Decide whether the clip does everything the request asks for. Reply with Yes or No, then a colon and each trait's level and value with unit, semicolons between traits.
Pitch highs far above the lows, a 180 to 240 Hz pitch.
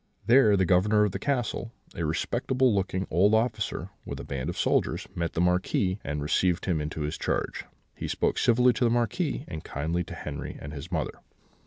No: wide, 5.8 semitones; very low, 95 Hz